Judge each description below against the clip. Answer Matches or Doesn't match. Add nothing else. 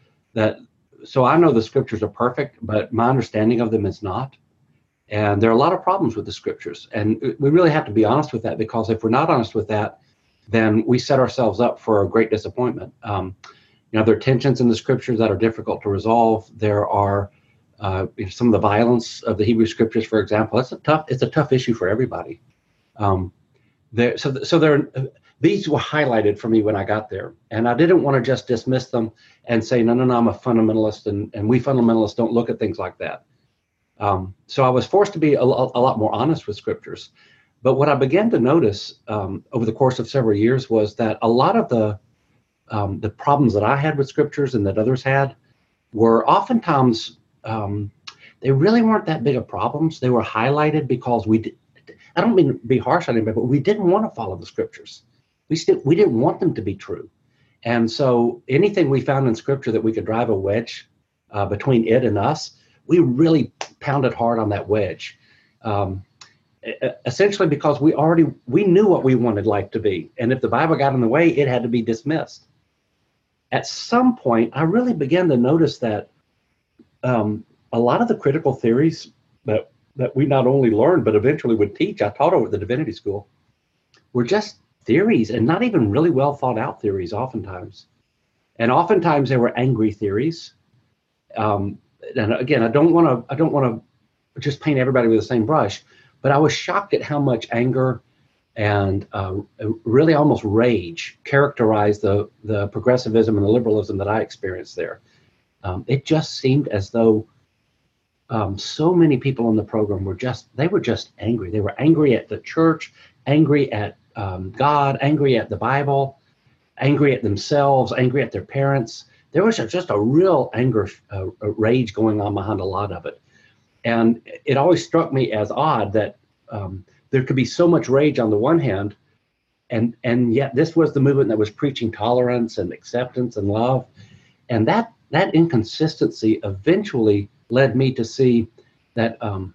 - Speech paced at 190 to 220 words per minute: Matches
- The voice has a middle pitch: Doesn't match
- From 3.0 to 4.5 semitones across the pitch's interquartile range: Matches